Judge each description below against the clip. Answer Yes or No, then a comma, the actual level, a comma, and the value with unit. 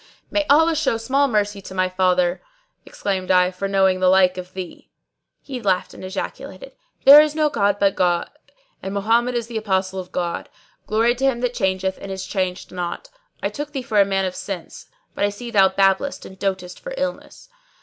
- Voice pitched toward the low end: No, high, 195 Hz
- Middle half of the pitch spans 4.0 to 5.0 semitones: Yes, average, 4.3 semitones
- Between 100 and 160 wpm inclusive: No, fast, 205 wpm